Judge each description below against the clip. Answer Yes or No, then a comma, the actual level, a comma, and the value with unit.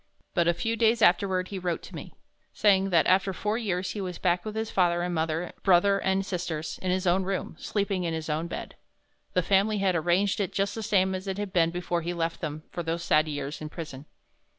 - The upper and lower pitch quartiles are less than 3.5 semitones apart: Yes, narrow, 2.6 semitones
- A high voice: No, medium, 180 Hz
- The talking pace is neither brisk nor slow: No, fast, 230 wpm